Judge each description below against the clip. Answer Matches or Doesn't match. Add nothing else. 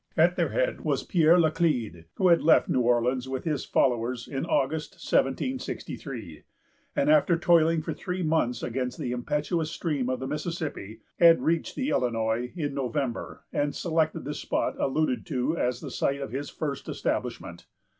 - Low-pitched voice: Doesn't match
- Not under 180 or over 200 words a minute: Doesn't match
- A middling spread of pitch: Matches